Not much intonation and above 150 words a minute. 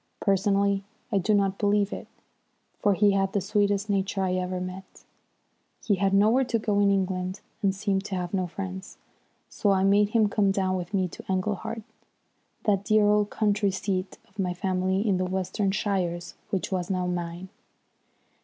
Yes: narrow, 1.6 semitones; average, 180 wpm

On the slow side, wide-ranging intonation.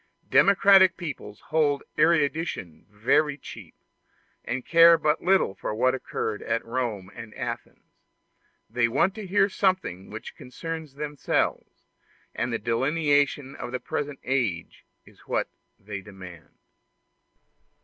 Yes: slow, 120 wpm; wide, 6.5 semitones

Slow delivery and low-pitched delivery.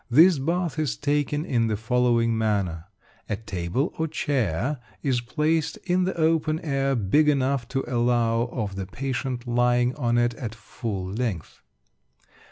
No: average, 150 wpm; low, 125 Hz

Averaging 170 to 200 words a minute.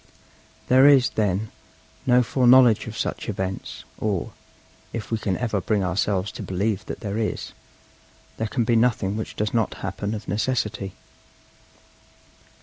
No: average, 145 wpm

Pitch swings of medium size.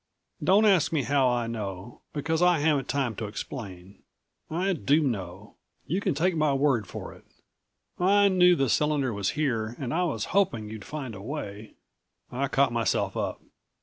No: wide, 6.4 semitones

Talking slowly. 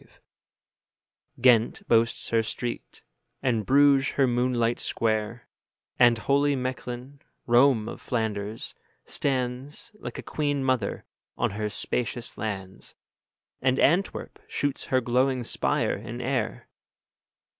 Yes: slow, 110 wpm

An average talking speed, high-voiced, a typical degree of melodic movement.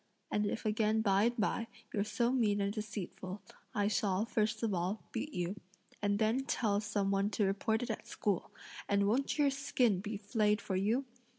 No: average, 190 wpm; high, 210 Hz; narrow, 2.1 semitones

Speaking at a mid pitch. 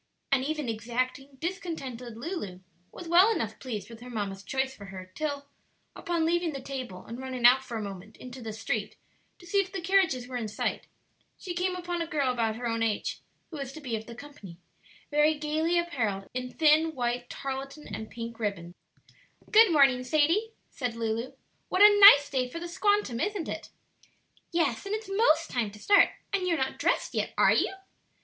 No: very high, 270 Hz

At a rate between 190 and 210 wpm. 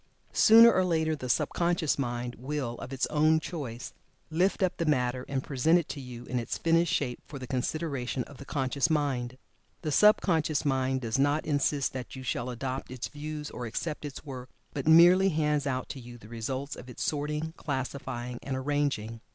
Yes: average, 195 wpm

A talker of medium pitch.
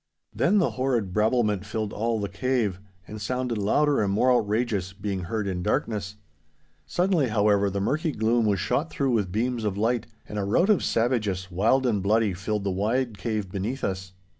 No: low, 110 Hz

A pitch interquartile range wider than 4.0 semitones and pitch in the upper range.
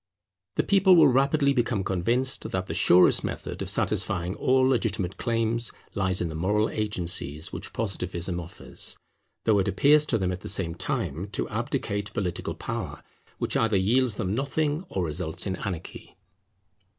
No: average, 5.3 semitones; low, 100 Hz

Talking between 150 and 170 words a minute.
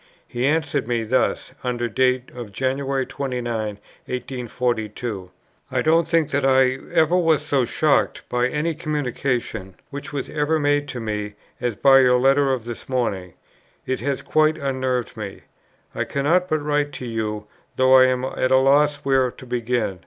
Yes: average, 165 wpm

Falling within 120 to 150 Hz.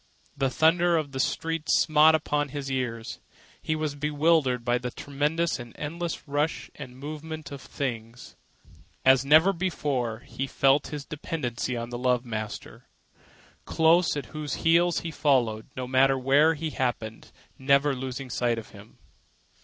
Yes: medium, 140 Hz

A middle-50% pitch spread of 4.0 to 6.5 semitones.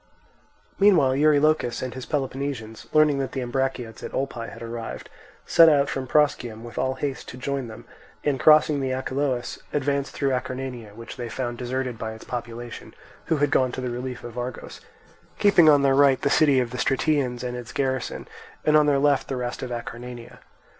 No: average, 2.7 semitones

